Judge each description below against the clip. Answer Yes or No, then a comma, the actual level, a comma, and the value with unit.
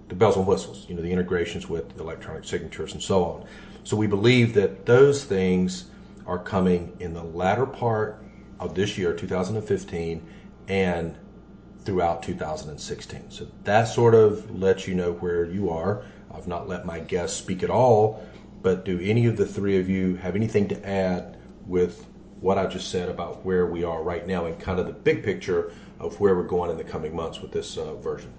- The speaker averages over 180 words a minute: Yes, average, 195 wpm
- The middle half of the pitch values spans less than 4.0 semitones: Yes, average, 3.3 semitones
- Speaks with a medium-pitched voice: No, very low, 95 Hz